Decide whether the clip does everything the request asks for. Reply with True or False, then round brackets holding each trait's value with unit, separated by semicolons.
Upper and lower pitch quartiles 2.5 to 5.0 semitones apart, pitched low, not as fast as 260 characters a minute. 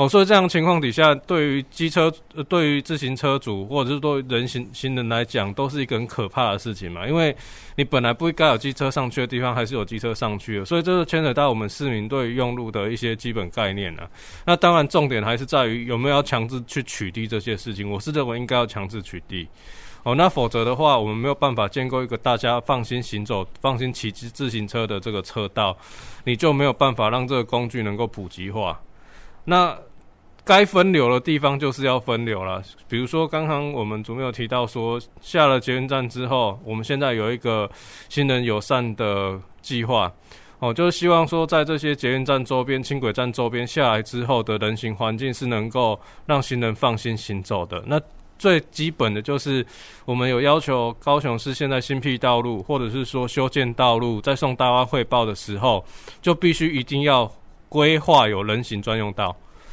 False (4.0 semitones; 125 Hz; 310 characters per minute)